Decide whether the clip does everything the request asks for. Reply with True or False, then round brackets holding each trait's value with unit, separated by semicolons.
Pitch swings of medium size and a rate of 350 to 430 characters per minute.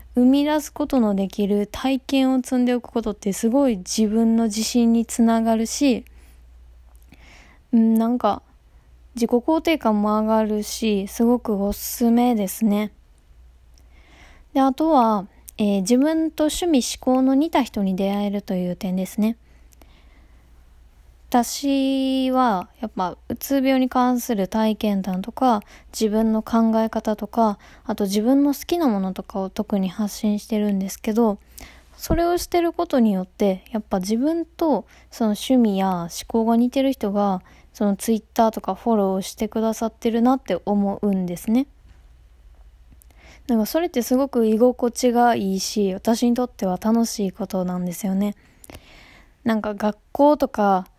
False (4.3 semitones; 285 characters per minute)